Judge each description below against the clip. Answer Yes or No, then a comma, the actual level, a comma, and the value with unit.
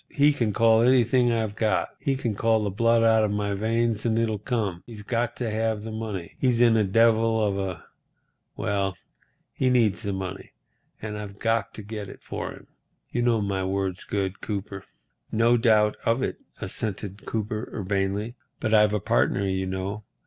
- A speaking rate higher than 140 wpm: Yes, average, 180 wpm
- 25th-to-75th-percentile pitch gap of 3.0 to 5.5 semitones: No, narrow, 2.4 semitones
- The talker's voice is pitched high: No, low, 110 Hz